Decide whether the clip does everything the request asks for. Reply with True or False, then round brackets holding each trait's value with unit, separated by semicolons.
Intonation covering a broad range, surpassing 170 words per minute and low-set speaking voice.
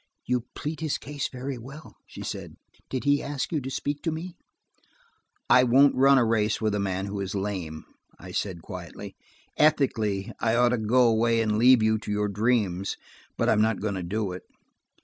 False (4.5 semitones; 200 wpm; 115 Hz)